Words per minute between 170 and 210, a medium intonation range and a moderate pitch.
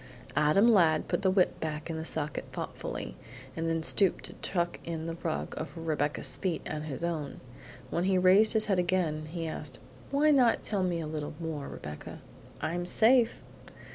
Yes: average, 180 wpm; average, 3.3 semitones; medium, 165 Hz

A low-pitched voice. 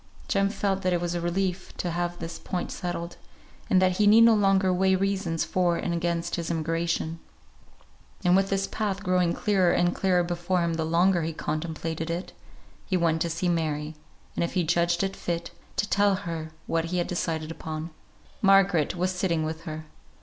No: medium, 175 Hz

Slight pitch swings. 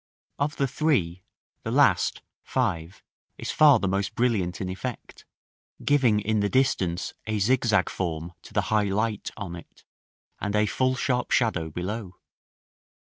No: average, 5.3 semitones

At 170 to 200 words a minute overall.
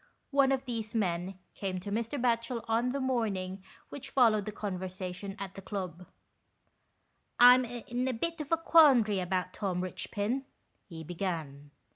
No: average, 150 wpm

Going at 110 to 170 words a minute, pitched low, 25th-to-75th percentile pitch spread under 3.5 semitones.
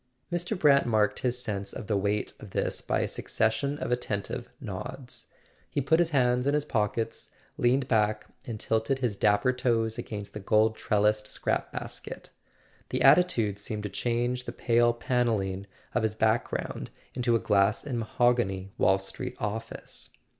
Yes: average, 160 wpm; low, 115 Hz; average, 3.0 semitones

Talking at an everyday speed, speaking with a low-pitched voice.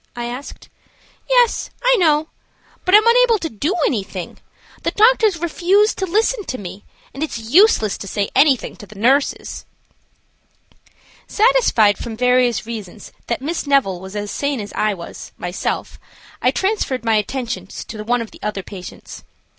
No: average, 160 wpm; very high, 250 Hz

